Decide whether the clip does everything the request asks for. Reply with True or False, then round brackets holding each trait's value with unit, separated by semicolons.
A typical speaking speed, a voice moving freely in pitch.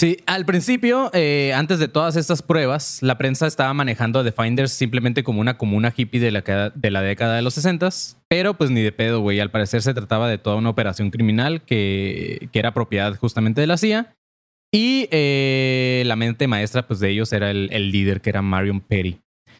False (210 wpm; 5.9 semitones)